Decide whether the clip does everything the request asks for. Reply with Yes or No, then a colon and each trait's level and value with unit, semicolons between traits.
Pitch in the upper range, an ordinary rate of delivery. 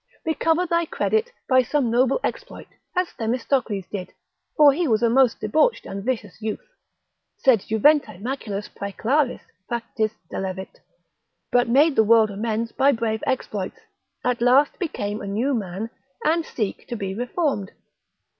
Yes: high, 235 Hz; average, 145 wpm